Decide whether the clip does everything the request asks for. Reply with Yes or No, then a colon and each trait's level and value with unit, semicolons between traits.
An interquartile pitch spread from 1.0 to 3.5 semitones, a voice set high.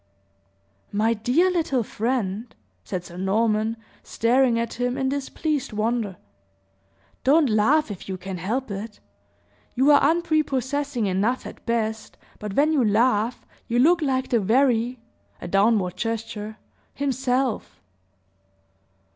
No: average, 4.1 semitones; high, 235 Hz